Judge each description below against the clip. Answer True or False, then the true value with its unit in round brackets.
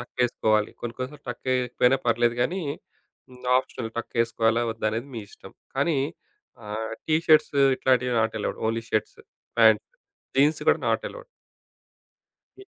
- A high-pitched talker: False (120 Hz)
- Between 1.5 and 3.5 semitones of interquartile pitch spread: True (2.9 semitones)